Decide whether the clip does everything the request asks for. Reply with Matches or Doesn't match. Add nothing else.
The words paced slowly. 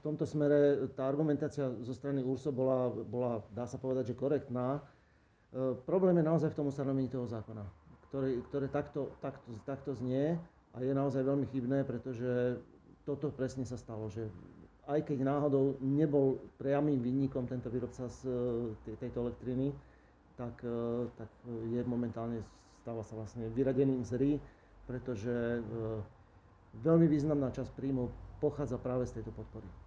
Doesn't match